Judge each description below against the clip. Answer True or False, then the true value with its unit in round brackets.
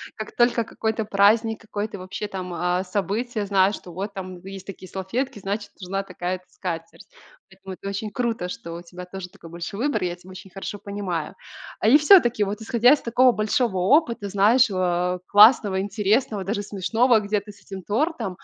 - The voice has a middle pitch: False (200 Hz)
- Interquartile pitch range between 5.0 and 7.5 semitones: False (3.2 semitones)